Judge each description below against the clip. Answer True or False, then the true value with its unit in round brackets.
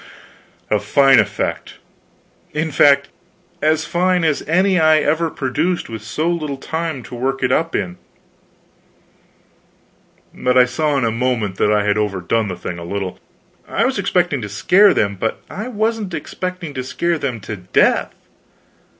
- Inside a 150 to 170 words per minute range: True (160 wpm)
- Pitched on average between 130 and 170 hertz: True (140 Hz)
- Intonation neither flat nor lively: False (7.2 semitones)